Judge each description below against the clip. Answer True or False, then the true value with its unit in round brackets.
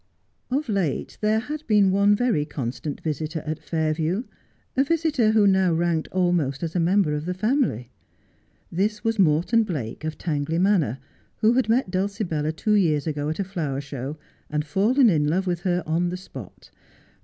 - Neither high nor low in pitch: True (175 Hz)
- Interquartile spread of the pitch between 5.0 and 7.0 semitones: True (5.3 semitones)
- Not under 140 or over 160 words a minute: False (170 wpm)